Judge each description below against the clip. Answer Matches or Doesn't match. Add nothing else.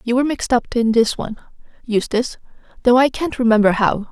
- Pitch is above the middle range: Matches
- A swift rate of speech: Doesn't match